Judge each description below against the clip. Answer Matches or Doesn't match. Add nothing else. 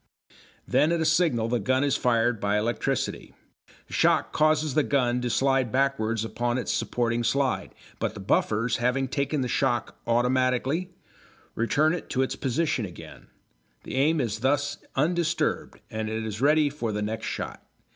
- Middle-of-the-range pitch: Doesn't match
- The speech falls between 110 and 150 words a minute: Doesn't match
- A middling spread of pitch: Matches